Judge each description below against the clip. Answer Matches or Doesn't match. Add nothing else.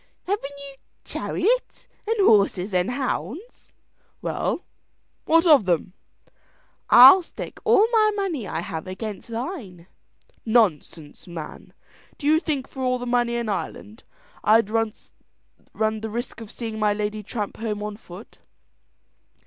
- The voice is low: Doesn't match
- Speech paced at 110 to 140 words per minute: Matches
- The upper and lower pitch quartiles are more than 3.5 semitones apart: Matches